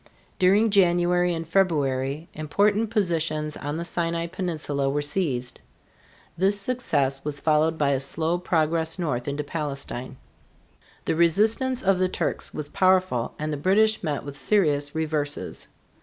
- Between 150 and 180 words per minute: No, average, 140 wpm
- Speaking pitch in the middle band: Yes, medium, 160 Hz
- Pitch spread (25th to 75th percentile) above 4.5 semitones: No, average, 4.2 semitones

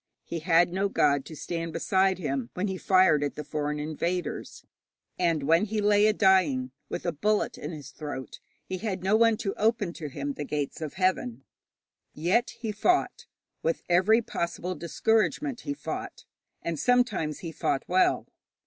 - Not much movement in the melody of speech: No, average, 5.3 semitones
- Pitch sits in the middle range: Yes, medium, 175 Hz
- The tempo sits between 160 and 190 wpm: Yes, average, 170 wpm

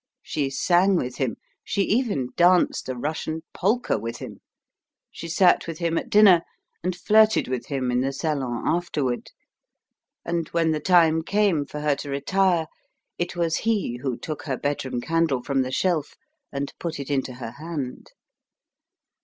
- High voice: No, medium, 160 Hz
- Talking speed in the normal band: Yes, average, 160 wpm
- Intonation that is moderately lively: Yes, average, 4.5 semitones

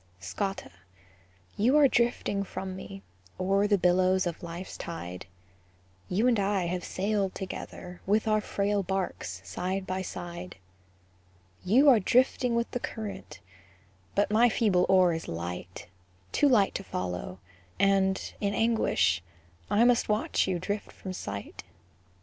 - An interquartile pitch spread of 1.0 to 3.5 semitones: Yes, average, 3.0 semitones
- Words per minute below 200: Yes, average, 140 wpm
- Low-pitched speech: No, high, 195 Hz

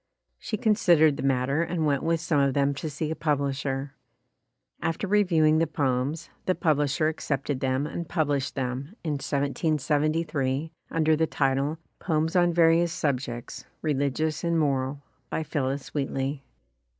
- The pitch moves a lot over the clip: No, average, 2.8 semitones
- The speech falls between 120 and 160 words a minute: Yes, average, 145 wpm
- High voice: No, medium, 150 Hz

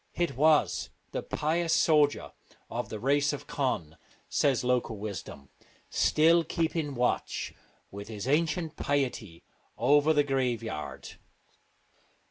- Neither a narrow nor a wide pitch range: Yes, average, 4.9 semitones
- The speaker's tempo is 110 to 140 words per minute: Yes, slow, 135 wpm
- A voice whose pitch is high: No, medium, 140 Hz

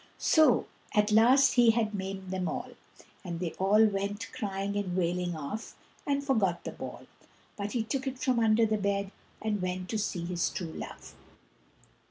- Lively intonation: No, average, 3.3 semitones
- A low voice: No, high, 205 Hz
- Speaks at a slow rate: No, average, 175 wpm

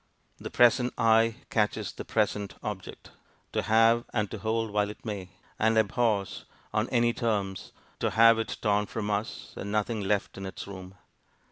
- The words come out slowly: No, average, 165 wpm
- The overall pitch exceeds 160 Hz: No, low, 110 Hz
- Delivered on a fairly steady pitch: Yes, narrow, 2.0 semitones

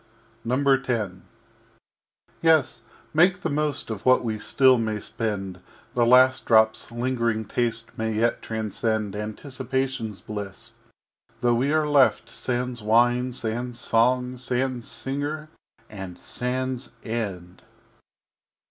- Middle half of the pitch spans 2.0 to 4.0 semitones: Yes, average, 2.9 semitones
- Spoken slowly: Yes, slow, 110 wpm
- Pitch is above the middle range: No, low, 120 Hz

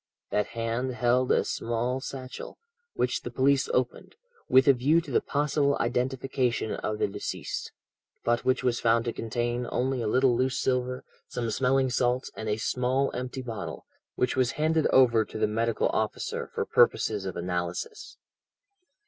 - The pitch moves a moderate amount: No, narrow, 2.2 semitones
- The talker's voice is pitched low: Yes, low, 125 Hz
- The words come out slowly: No, average, 160 wpm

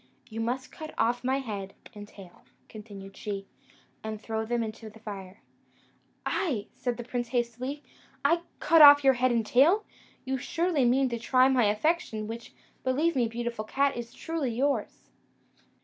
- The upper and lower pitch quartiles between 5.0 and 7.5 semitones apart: No, average, 3.7 semitones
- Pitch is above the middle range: Yes, high, 240 Hz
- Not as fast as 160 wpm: No, average, 165 wpm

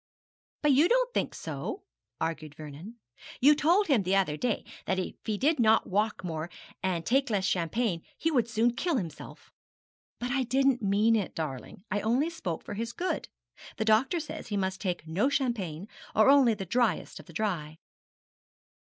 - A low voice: No, high, 220 Hz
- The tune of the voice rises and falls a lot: Yes, wide, 6.5 semitones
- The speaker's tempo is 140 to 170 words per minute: No, average, 180 wpm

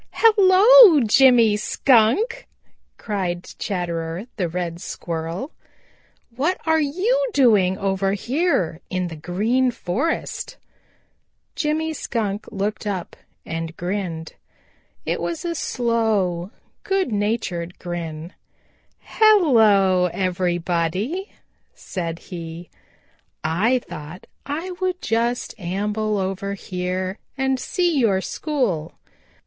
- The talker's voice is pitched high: Yes, high, 205 Hz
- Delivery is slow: Yes, slow, 95 wpm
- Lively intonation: Yes, wide, 7.7 semitones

